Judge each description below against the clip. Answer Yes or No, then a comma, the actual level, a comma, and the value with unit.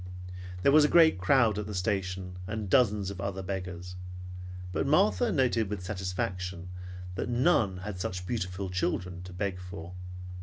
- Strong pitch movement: No, average, 3.3 semitones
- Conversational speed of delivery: Yes, average, 155 wpm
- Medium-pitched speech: No, very low, 95 Hz